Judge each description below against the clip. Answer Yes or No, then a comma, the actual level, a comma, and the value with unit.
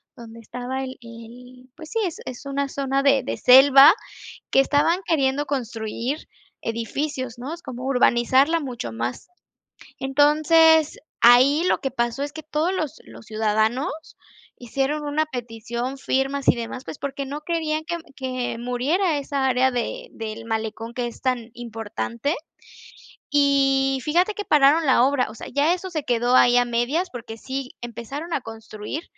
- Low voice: No, very high, 265 Hz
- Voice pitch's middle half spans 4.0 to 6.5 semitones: No, average, 3.5 semitones